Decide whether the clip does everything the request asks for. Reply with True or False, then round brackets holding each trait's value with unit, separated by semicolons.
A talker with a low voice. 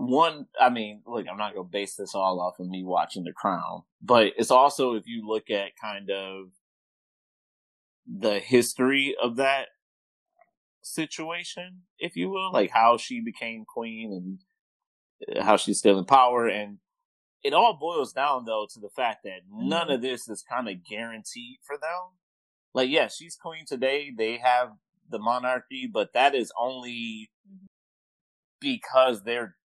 True (125 Hz)